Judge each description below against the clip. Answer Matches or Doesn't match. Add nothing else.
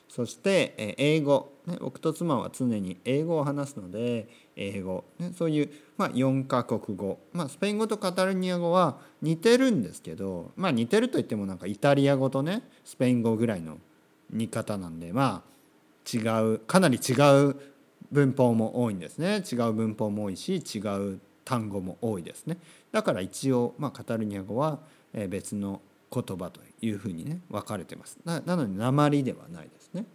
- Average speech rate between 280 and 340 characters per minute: Matches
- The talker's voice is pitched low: Matches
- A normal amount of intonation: Doesn't match